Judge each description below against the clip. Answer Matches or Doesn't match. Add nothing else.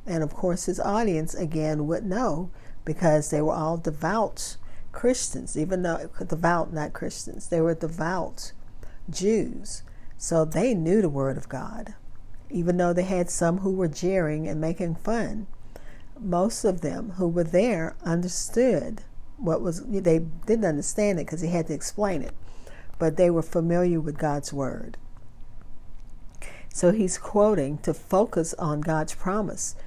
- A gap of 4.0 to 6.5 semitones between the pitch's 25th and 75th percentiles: Doesn't match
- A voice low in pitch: Doesn't match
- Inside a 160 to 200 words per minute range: Doesn't match